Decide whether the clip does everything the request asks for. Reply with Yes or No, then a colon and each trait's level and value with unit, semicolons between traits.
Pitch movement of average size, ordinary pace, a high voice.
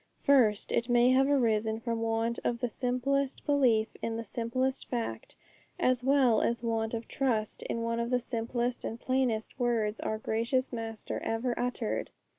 No: narrow, 2.1 semitones; average, 165 wpm; high, 235 Hz